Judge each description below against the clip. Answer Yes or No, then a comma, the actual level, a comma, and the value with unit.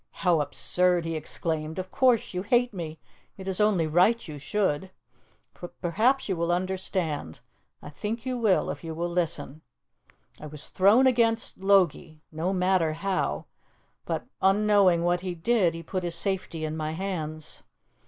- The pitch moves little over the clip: No, average, 3.5 semitones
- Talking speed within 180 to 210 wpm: No, average, 160 wpm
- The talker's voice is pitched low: No, medium, 180 Hz